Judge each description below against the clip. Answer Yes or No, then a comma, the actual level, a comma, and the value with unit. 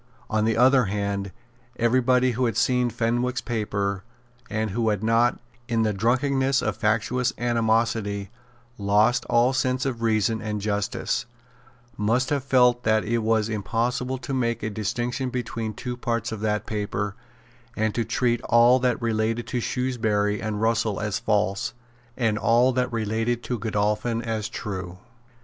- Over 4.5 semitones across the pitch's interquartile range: No, narrow, 2.5 semitones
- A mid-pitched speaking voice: No, low, 115 Hz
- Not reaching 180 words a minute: Yes, average, 155 wpm